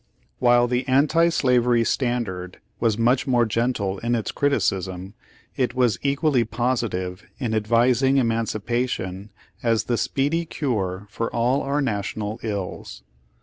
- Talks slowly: Yes, slow, 125 wpm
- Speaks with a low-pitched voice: Yes, low, 120 Hz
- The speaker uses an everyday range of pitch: Yes, average, 3.5 semitones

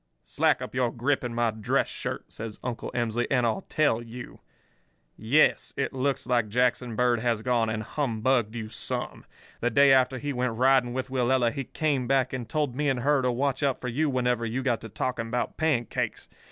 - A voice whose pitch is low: Yes, low, 125 Hz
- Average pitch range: No, narrow, 2.2 semitones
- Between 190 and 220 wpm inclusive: Yes, average, 200 wpm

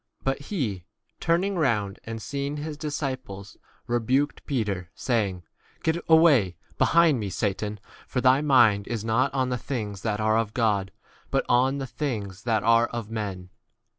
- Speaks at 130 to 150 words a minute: No, average, 165 wpm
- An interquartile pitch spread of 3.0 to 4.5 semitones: No, average, 5.0 semitones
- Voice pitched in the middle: No, low, 120 Hz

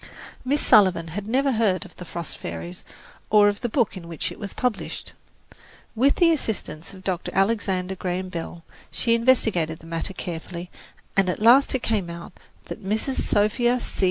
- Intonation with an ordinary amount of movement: Yes, average, 5.0 semitones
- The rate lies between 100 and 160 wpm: No, average, 175 wpm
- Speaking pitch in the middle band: No, high, 195 Hz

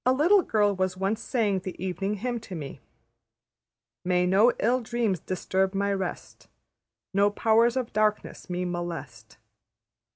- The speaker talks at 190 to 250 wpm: No, average, 140 wpm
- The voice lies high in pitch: Yes, high, 200 Hz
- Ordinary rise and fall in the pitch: Yes, average, 3.7 semitones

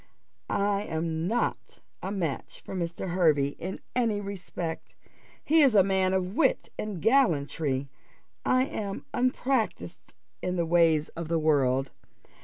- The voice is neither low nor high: Yes, medium, 180 Hz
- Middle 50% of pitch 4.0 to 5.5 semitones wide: Yes, average, 4.5 semitones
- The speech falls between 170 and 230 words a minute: No, slow, 135 wpm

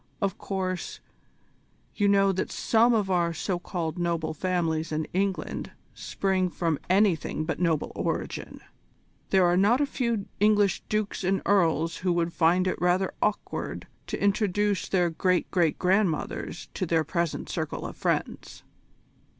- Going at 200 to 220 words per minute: No, average, 150 wpm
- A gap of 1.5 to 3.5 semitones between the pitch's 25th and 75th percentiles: Yes, average, 2.8 semitones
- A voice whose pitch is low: No, medium, 185 Hz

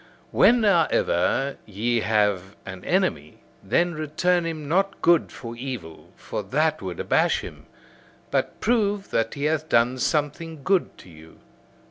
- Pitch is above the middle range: No, medium, 140 Hz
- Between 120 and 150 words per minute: Yes, average, 140 wpm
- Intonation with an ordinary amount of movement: No, wide, 7.7 semitones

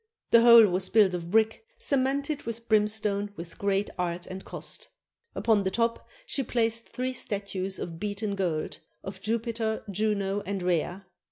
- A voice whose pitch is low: No, high, 210 Hz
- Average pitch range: Yes, average, 3.3 semitones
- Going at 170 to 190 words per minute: No, average, 155 wpm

